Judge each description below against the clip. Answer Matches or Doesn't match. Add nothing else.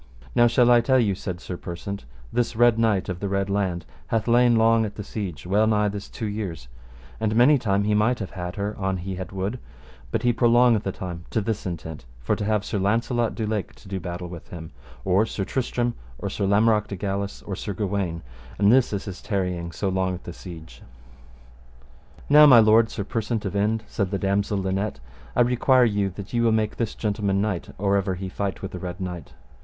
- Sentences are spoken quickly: Matches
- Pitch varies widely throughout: Doesn't match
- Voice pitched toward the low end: Matches